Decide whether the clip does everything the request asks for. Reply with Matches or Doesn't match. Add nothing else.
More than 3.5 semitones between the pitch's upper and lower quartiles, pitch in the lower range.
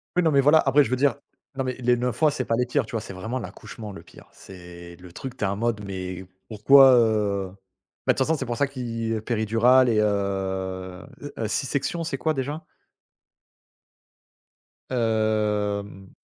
Matches